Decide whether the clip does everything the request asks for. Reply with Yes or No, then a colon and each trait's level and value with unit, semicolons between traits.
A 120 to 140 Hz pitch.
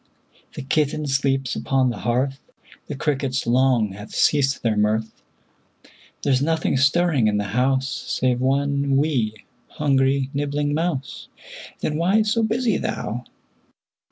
Yes: low, 135 Hz